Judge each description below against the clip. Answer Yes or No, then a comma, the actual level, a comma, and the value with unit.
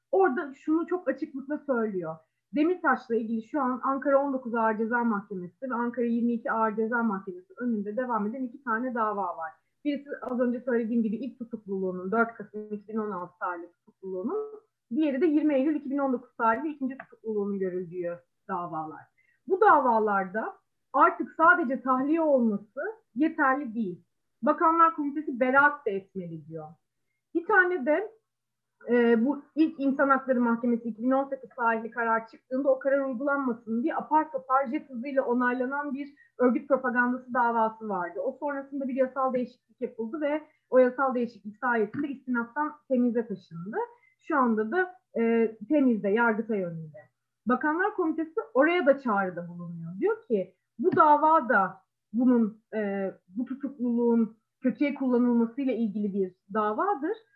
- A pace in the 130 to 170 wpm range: Yes, average, 135 wpm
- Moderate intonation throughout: Yes, average, 4.7 semitones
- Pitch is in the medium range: No, very high, 250 Hz